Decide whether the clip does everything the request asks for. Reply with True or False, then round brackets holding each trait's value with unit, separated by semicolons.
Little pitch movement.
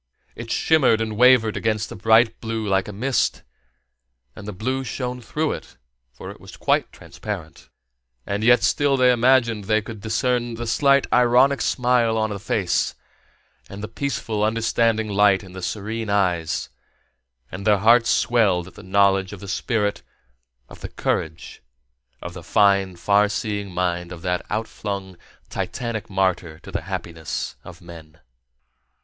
False (3.5 semitones)